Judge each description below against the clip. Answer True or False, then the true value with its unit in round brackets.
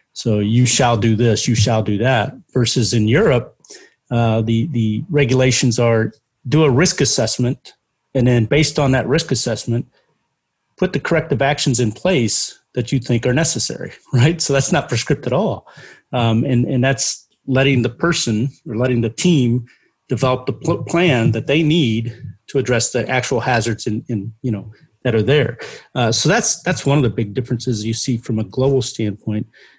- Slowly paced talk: False (180 wpm)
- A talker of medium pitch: False (125 Hz)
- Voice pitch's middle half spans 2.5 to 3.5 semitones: True (3.1 semitones)